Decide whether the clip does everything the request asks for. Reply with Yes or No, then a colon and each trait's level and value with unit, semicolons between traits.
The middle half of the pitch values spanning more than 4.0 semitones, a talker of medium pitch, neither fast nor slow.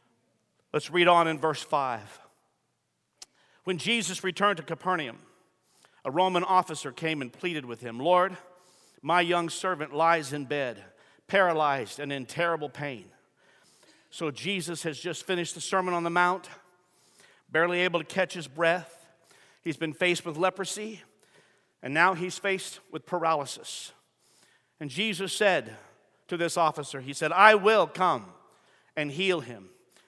No: average, 3.1 semitones; medium, 170 Hz; average, 145 wpm